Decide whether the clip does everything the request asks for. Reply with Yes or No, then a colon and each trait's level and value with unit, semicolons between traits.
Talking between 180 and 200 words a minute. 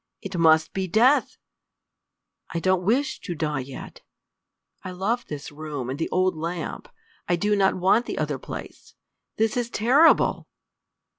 No: average, 150 wpm